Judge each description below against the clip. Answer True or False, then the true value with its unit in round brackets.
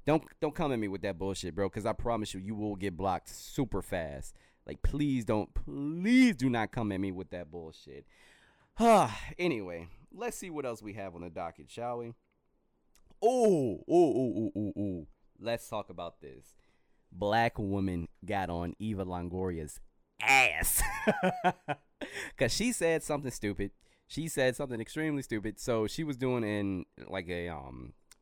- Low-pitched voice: True (110 Hz)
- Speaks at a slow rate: False (165 wpm)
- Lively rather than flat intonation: True (7.5 semitones)